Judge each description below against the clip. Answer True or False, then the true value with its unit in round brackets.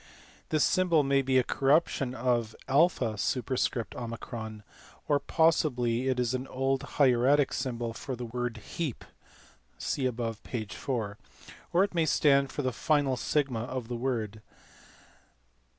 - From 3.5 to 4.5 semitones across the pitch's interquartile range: False (3.0 semitones)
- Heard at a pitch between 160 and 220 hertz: False (130 Hz)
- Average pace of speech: False (130 wpm)